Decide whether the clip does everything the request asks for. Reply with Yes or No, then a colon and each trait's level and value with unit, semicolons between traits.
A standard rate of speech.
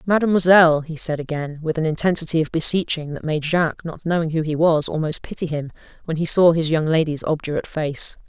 Yes: average, 190 wpm